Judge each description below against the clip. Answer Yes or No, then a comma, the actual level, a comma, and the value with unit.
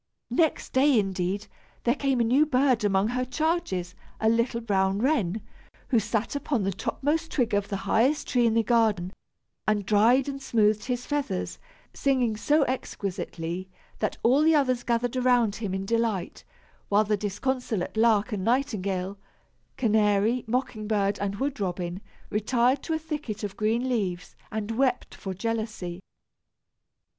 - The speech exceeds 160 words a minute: No, average, 150 wpm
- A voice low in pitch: No, high, 225 Hz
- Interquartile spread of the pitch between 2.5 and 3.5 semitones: No, average, 4.1 semitones